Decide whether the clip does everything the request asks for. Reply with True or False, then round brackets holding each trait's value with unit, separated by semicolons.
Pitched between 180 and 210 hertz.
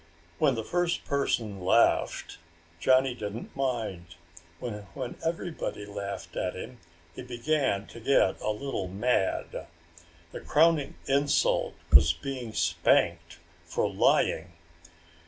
False (120 Hz)